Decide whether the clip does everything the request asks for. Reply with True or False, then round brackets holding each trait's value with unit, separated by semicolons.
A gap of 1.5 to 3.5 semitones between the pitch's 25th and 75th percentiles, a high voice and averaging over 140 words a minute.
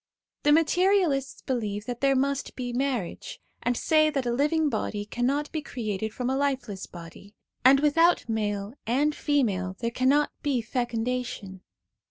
False (4.6 semitones; 255 Hz; 150 wpm)